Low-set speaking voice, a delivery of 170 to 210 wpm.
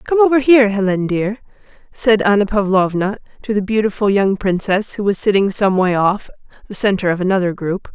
No: high, 205 Hz; average, 180 wpm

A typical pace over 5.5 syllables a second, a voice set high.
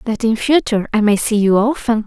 Yes: 5.8 syllables/s; high, 220 Hz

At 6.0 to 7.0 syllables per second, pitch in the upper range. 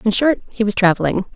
Yes: 6.4 syllables/s; high, 210 Hz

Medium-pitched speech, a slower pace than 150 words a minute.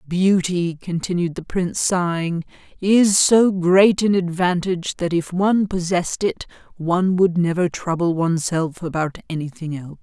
Yes: medium, 175 Hz; average, 140 wpm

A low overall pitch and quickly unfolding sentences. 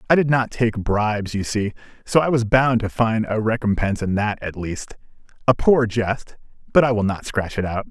Yes: low, 110 Hz; fast, 220 wpm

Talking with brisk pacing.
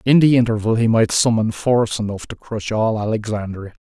No: average, 190 wpm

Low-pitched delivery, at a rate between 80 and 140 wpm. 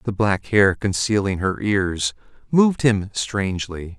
Yes: low, 100 Hz; slow, 135 wpm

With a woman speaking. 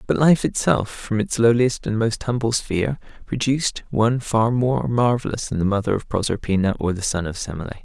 No: male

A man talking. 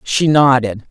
No: female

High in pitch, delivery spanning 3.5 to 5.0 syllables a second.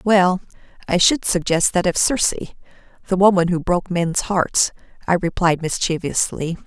No: medium, 180 Hz; 4.9 syllables/s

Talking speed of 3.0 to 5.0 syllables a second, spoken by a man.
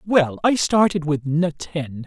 Yes: 3.7 syllables/s; male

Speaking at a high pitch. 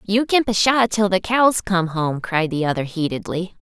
Yes: high, 195 Hz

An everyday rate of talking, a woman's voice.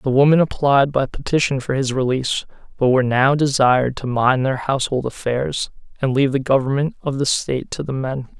No: average, 195 wpm; male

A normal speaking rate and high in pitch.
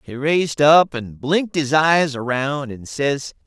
No: average, 175 wpm; medium, 145 Hz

